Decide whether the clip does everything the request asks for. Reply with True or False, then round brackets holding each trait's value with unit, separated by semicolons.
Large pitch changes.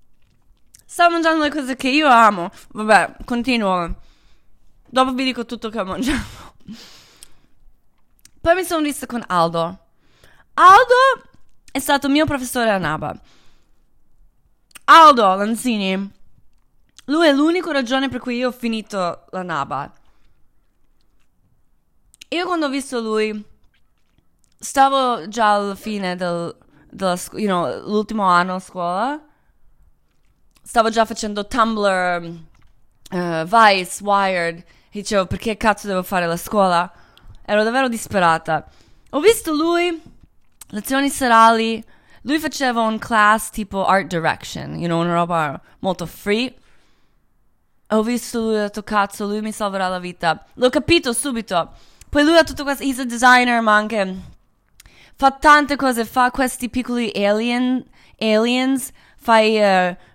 True (5.8 semitones)